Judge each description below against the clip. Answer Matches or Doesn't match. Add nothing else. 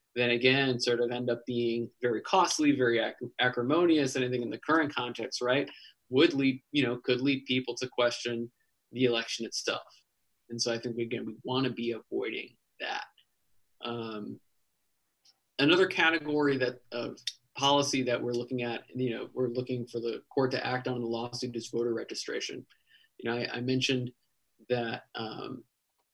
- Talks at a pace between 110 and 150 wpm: Doesn't match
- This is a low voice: Matches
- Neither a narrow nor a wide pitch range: Doesn't match